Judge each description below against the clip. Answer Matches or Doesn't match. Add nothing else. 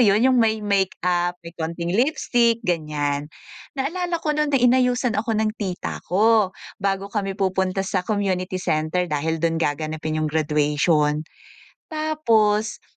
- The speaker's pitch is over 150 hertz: Matches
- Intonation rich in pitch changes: Matches